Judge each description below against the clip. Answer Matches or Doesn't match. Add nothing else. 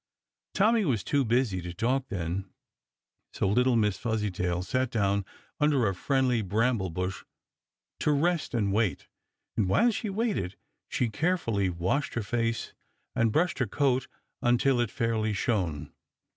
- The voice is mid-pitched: Doesn't match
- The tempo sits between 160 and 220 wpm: Doesn't match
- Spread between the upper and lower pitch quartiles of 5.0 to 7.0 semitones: Matches